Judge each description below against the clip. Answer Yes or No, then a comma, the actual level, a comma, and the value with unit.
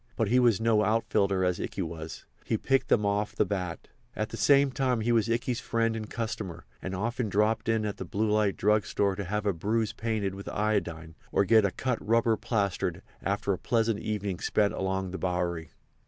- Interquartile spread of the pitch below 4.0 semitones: Yes, average, 2.9 semitones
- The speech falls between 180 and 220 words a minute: Yes, fast, 205 wpm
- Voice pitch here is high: No, low, 105 Hz